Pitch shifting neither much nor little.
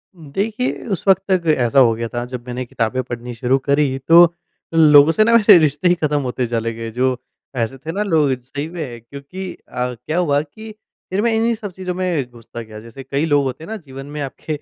No: wide, 6.0 semitones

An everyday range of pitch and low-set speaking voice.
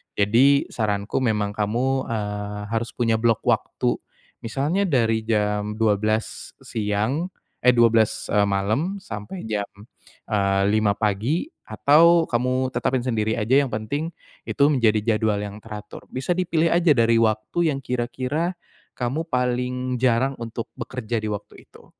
Yes: average, 3.6 semitones; low, 115 Hz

